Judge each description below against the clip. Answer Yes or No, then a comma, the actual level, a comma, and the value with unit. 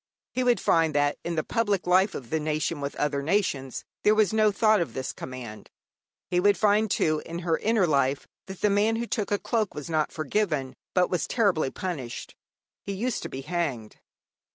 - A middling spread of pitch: No, wide, 6.1 semitones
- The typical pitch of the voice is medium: Yes, medium, 175 Hz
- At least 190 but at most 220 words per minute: Yes, average, 200 wpm